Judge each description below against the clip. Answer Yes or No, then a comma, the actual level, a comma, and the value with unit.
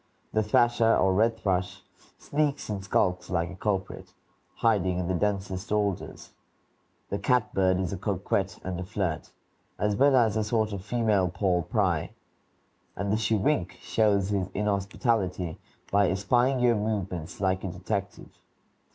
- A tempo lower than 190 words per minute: Yes, average, 145 wpm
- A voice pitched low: Yes, low, 100 Hz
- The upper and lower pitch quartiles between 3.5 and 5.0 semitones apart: No, average, 2.8 semitones